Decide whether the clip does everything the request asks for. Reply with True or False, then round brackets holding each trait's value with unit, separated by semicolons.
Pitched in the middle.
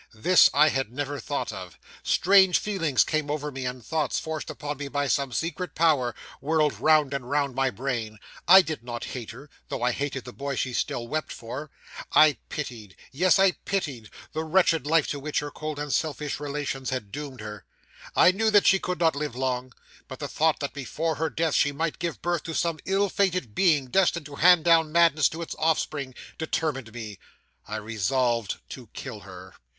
True (145 Hz)